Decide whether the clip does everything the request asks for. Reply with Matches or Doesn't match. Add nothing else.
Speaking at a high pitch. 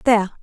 Matches